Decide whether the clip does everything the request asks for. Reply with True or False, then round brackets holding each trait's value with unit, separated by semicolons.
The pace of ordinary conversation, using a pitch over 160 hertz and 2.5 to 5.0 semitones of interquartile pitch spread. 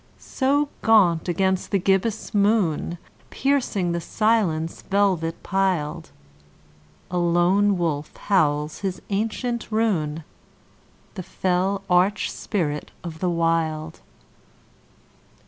False (95 wpm; 185 Hz; 3.7 semitones)